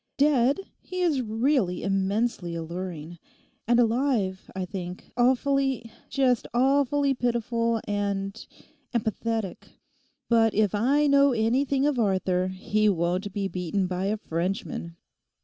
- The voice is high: Yes, high, 220 Hz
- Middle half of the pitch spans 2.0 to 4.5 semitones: No, wide, 5.6 semitones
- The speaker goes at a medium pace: No, slow, 115 wpm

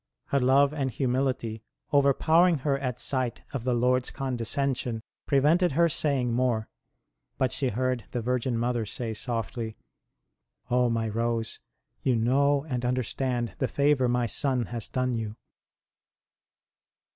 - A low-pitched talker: Yes, low, 125 Hz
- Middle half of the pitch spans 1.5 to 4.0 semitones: Yes, average, 2.8 semitones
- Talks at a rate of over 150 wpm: No, average, 140 wpm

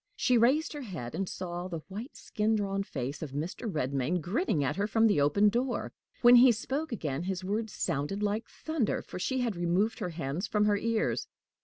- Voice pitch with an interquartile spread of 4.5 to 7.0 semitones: Yes, average, 5.3 semitones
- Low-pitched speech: No, high, 200 Hz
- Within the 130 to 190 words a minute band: No, average, 200 wpm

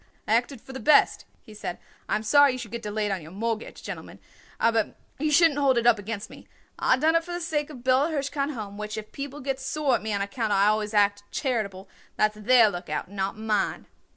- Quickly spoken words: Yes, fast, 235 wpm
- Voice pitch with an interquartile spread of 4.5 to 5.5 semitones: Yes, average, 4.8 semitones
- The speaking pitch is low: No, high, 230 Hz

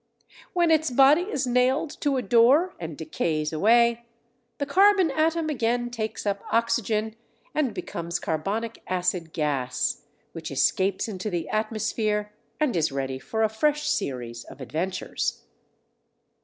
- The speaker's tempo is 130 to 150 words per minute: Yes, slow, 135 wpm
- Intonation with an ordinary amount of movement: No, wide, 7.6 semitones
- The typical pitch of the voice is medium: No, high, 220 Hz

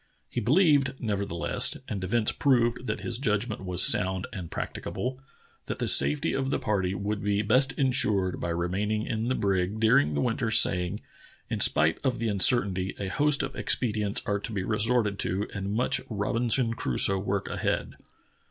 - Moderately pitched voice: No, low, 105 Hz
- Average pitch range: Yes, average, 4.0 semitones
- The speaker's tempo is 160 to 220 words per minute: Yes, average, 170 wpm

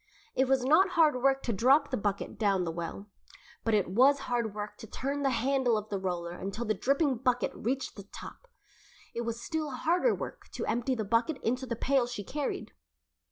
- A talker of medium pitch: No, high, 245 Hz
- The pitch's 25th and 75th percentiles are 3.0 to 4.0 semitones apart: No, average, 4.4 semitones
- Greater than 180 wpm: Yes, fast, 205 wpm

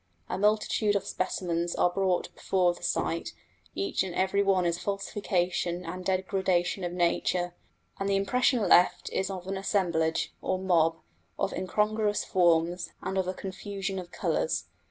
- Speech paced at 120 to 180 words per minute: Yes, average, 155 wpm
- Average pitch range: No, narrow, 2.0 semitones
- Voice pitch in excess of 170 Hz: Yes, medium, 185 Hz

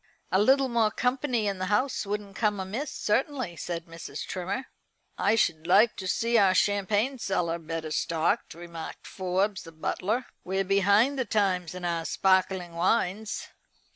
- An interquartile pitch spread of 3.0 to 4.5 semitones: Yes, average, 3.8 semitones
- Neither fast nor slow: Yes, average, 155 wpm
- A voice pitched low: No, high, 195 Hz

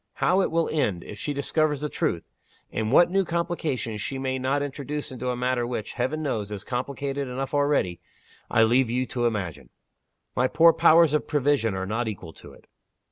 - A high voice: No, low, 130 Hz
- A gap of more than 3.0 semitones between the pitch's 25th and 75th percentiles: Yes, average, 4.6 semitones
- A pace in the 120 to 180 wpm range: No, average, 190 wpm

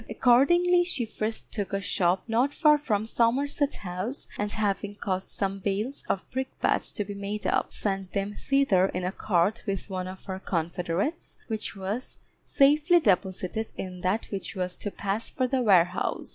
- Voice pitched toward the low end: No, high, 205 Hz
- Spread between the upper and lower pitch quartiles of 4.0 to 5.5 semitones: Yes, average, 4.9 semitones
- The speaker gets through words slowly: No, average, 175 wpm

